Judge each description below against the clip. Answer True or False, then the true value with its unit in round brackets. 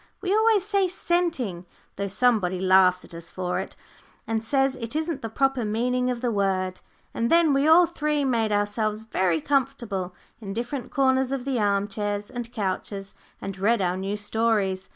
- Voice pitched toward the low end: False (225 Hz)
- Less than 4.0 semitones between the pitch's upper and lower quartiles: False (5.6 semitones)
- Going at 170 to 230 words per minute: True (175 wpm)